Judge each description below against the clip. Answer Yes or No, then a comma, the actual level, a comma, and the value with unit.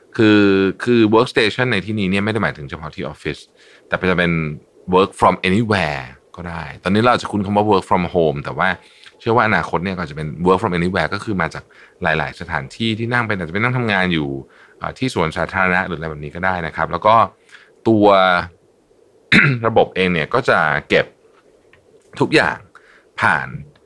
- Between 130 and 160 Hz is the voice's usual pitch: No, very low, 95 Hz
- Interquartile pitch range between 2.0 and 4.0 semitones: No, average, 4.6 semitones